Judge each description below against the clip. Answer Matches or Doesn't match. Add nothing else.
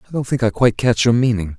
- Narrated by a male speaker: Matches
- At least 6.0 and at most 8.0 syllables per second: Matches